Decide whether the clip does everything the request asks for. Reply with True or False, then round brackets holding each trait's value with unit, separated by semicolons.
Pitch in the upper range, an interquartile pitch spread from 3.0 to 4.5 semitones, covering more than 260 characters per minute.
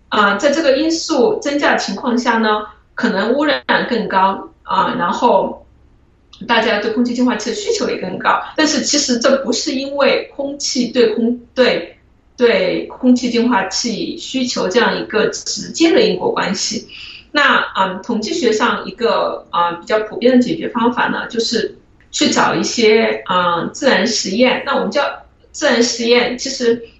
False (240 Hz; 4.0 semitones; 255 characters per minute)